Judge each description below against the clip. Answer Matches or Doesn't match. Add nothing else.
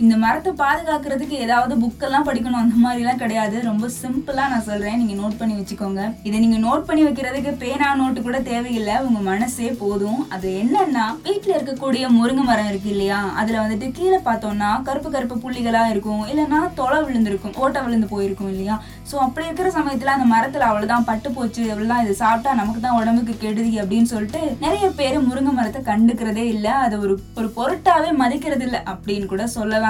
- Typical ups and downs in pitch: Matches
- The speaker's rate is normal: Doesn't match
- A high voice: Matches